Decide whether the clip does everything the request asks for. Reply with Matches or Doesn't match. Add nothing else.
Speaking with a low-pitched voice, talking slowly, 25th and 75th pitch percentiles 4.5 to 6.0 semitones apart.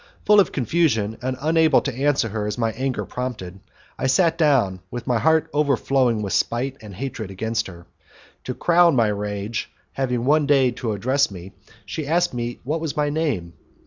Doesn't match